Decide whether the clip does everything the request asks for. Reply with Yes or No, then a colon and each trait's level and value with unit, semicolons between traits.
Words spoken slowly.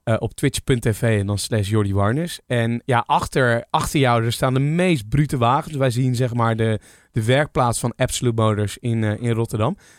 No: fast, 200 wpm